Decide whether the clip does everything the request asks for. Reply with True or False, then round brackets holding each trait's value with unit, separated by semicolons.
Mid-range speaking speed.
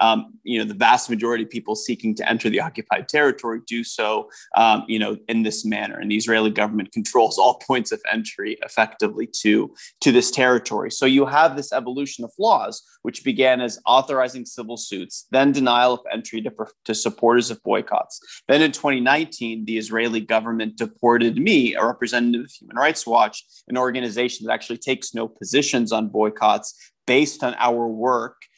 True (180 wpm)